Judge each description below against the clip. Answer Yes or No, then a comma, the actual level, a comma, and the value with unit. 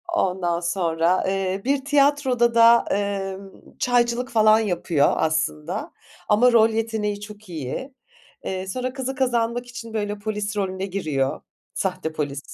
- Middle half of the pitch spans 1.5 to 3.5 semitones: No, average, 4.2 semitones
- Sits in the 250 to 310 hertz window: No, high, 205 Hz